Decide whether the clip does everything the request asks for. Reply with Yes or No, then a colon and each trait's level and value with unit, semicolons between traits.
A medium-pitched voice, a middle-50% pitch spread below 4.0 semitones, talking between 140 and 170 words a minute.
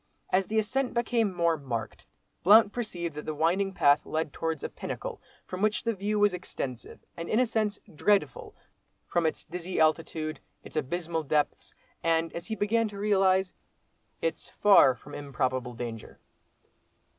No: medium, 175 Hz; average, 5.1 semitones; average, 150 wpm